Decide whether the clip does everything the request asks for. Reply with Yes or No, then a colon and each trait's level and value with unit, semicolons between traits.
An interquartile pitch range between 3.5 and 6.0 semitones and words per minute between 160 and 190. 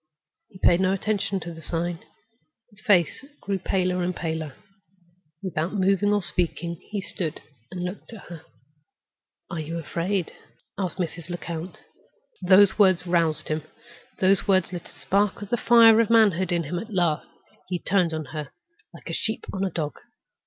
No: average, 2.8 semitones; average, 165 wpm